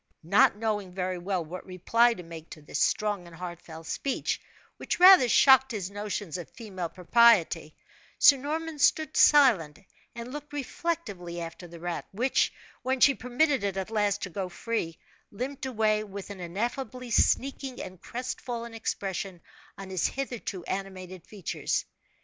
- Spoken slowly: No, average, 155 wpm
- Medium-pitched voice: No, high, 205 Hz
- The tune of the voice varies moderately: No, wide, 5.7 semitones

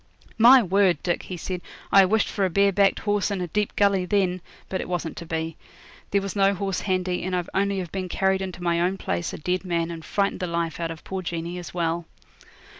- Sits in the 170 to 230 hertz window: Yes, medium, 185 Hz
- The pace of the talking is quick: Yes, fast, 235 wpm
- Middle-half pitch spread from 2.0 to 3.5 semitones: Yes, narrow, 2.4 semitones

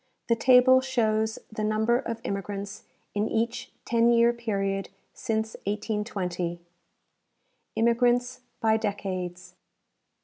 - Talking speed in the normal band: No, slow, 100 wpm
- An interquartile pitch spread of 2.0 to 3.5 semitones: Yes, average, 2.8 semitones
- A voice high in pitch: Yes, high, 220 Hz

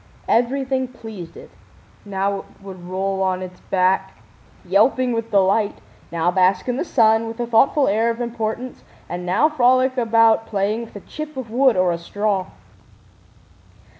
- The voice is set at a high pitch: Yes, high, 220 Hz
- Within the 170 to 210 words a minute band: No, average, 160 wpm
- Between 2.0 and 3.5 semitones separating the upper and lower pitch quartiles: No, average, 4.2 semitones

